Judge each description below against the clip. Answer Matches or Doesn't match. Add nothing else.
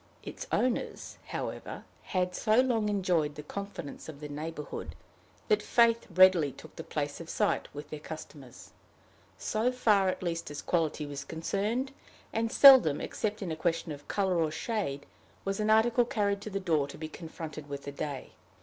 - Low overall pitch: Doesn't match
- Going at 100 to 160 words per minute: Doesn't match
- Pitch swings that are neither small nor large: Doesn't match